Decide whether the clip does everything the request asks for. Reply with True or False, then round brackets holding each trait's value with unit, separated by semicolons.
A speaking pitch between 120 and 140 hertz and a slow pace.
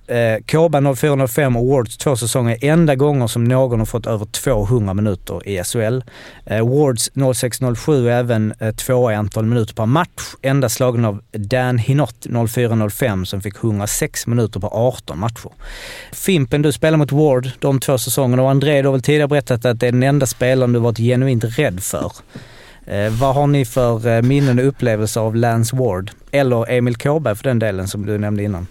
False (125 Hz; 180 wpm)